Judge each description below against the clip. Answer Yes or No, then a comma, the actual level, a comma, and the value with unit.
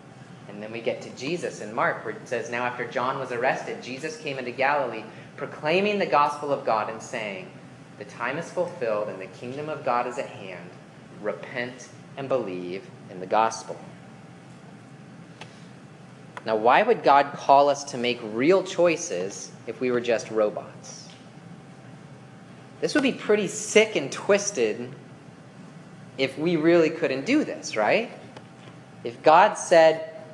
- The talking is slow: No, average, 150 wpm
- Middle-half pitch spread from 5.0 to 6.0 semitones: Yes, wide, 5.6 semitones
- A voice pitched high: No, medium, 145 Hz